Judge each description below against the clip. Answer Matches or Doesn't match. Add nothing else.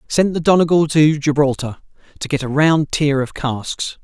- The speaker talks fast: Doesn't match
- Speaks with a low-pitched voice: Doesn't match